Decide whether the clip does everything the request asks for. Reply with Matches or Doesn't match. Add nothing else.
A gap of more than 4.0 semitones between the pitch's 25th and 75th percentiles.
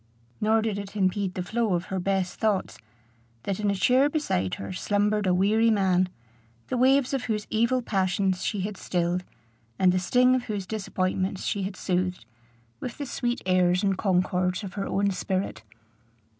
Doesn't match